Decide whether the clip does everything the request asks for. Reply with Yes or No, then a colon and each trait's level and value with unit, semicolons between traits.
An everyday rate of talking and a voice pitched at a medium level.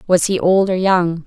No: fast, 240 wpm; medium, 180 Hz